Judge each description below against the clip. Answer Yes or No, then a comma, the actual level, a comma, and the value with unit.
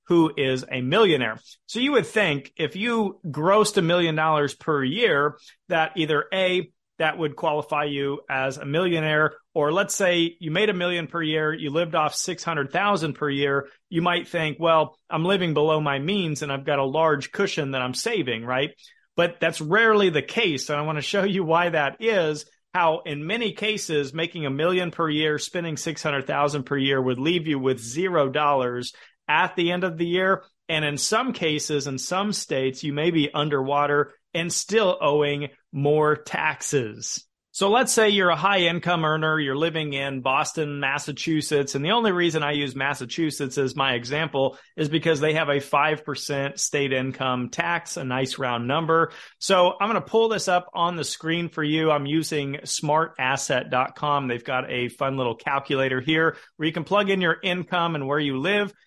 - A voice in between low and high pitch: Yes, medium, 155 Hz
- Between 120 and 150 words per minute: No, average, 190 wpm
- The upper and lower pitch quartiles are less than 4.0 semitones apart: Yes, average, 3.5 semitones